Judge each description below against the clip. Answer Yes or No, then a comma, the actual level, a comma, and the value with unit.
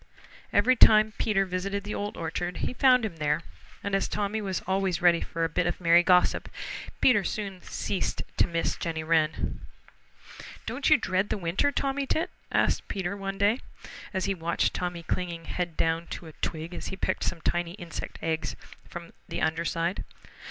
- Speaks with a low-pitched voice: No, medium, 180 Hz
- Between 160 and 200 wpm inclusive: Yes, average, 180 wpm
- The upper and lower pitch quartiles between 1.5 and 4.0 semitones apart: Yes, average, 3.3 semitones